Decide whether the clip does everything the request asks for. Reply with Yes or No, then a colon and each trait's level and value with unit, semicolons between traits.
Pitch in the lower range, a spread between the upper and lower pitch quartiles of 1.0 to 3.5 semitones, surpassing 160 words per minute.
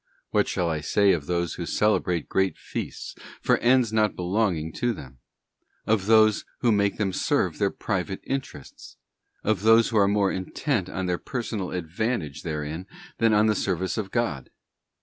No: low, 100 Hz; average, 4.1 semitones; average, 170 wpm